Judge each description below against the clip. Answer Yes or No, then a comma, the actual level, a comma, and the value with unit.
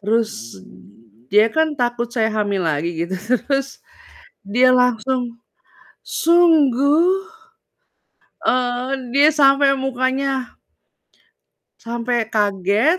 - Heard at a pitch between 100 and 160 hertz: No, very high, 250 Hz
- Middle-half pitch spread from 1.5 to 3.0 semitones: No, average, 4.0 semitones